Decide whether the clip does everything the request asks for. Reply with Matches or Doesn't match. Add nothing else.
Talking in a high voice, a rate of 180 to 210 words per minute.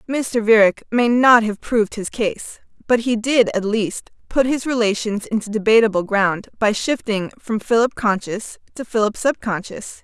Doesn't match